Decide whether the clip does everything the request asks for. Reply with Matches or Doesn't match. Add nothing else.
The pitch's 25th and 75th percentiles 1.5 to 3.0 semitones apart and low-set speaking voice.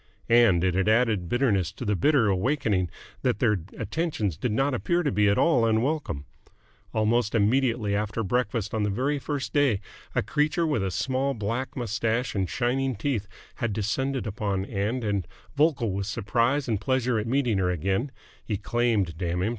Doesn't match